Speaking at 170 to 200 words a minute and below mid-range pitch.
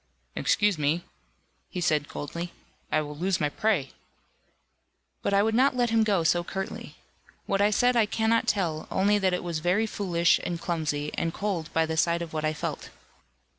No: average, 185 wpm; medium, 175 Hz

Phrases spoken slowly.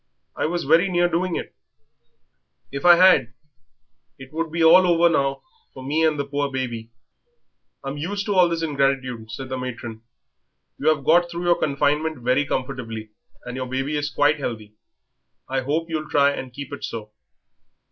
No: average, 175 wpm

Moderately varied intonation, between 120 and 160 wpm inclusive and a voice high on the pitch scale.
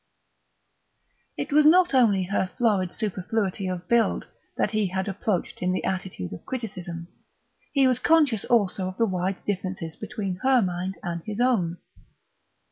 Yes: average, 4.4 semitones; average, 150 wpm; high, 195 Hz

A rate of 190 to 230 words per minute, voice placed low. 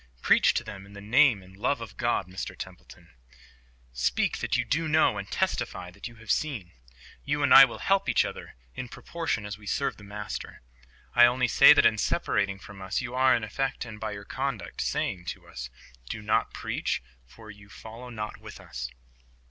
Yes: average, 200 wpm; low, 105 Hz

